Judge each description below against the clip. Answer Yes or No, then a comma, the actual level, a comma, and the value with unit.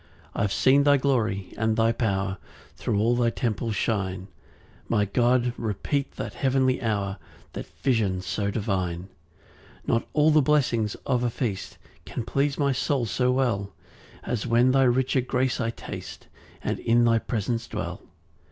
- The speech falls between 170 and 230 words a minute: No, average, 160 wpm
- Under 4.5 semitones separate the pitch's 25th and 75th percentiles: Yes, average, 4.0 semitones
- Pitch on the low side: Yes, low, 115 Hz